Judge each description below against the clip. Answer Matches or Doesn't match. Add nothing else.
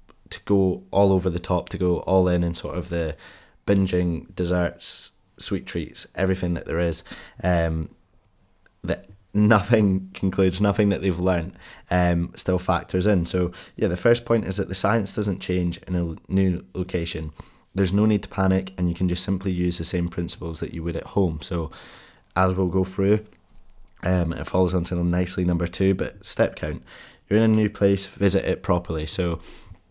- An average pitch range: Doesn't match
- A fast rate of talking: Doesn't match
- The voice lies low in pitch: Matches